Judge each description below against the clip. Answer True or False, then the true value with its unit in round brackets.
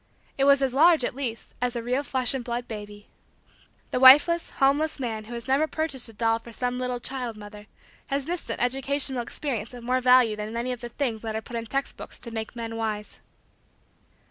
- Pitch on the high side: True (245 Hz)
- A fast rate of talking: True (215 wpm)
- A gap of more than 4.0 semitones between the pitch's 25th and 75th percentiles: False (3.0 semitones)